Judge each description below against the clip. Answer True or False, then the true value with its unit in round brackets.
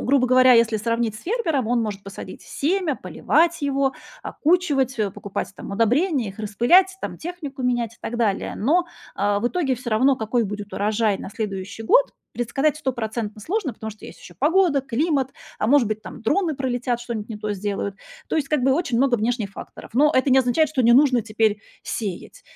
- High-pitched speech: True (245 Hz)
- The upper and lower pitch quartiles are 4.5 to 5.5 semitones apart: True (4.9 semitones)